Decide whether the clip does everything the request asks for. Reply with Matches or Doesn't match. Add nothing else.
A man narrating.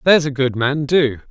Matches